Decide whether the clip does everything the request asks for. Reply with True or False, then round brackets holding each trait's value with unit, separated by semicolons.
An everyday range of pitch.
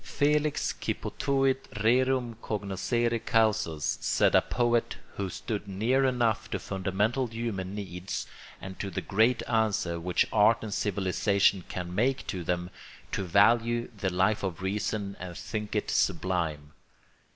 True (3.8 semitones)